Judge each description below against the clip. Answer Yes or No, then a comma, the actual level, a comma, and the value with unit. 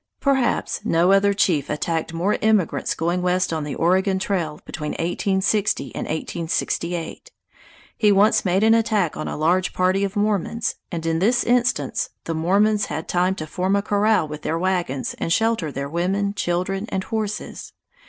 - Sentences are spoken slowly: No, average, 165 wpm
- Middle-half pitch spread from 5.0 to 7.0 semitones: No, average, 3.8 semitones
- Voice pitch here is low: No, medium, 185 Hz